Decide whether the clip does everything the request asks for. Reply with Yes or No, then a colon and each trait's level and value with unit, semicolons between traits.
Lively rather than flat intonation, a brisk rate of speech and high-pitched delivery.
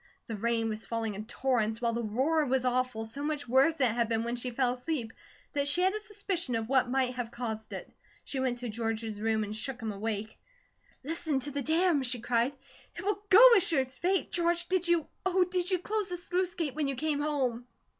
Yes: wide, 6.1 semitones; fast, 230 wpm; very high, 260 Hz